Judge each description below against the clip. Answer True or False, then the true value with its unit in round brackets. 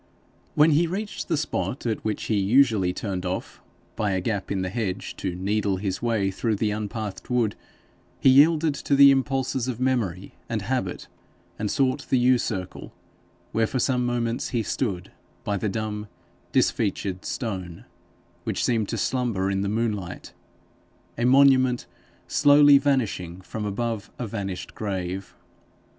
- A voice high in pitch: False (110 Hz)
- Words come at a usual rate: True (150 wpm)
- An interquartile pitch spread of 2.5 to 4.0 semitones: False (4.7 semitones)